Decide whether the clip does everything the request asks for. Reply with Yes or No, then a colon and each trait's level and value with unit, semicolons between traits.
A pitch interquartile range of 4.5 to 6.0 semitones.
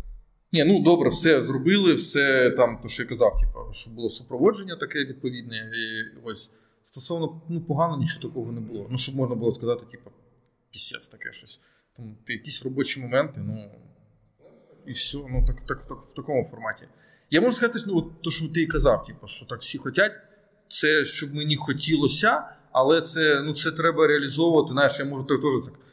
Yes: average, 5.1 semitones